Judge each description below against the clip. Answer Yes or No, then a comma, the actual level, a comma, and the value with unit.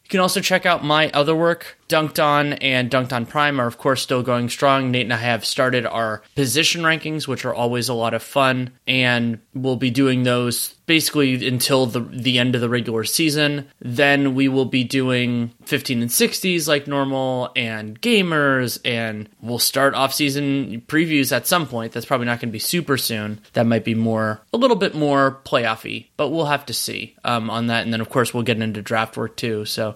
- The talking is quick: Yes, fast, 210 wpm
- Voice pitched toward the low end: Yes, low, 130 Hz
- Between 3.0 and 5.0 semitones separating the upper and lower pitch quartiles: Yes, average, 3.5 semitones